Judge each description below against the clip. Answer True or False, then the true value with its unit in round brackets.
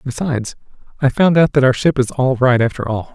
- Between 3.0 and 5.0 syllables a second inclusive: False (6.2 syllables/s)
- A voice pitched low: True (130 Hz)